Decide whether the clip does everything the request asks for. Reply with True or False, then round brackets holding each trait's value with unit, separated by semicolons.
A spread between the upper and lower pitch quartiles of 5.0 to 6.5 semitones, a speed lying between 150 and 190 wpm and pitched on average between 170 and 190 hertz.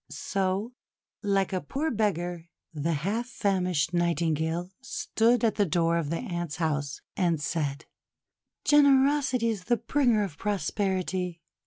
False (5.4 semitones; 135 wpm; 185 Hz)